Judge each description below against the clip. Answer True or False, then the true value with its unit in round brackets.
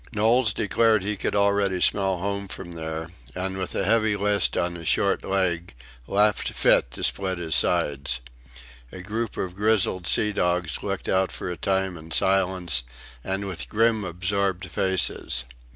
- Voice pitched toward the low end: True (95 Hz)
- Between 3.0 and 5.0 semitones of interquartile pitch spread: False (2.5 semitones)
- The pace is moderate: True (160 wpm)